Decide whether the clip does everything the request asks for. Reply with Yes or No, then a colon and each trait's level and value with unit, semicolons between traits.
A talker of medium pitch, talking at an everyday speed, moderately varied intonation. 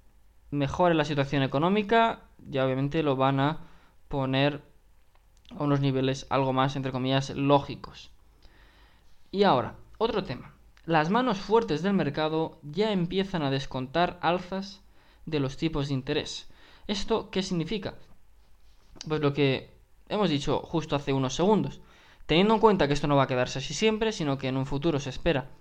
Yes: medium, 145 Hz; average, 155 wpm; average, 4.7 semitones